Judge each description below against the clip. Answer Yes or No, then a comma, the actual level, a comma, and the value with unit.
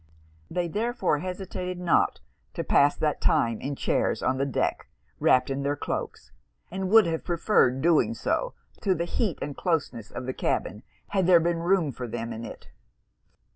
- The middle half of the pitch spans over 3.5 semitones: Yes, average, 5.3 semitones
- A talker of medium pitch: Yes, medium, 165 Hz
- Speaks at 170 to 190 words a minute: Yes, average, 175 wpm